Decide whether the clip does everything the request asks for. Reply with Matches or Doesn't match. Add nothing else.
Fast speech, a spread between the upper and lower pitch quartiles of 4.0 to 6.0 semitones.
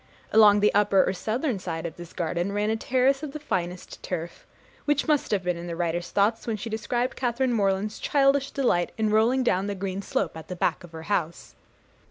Matches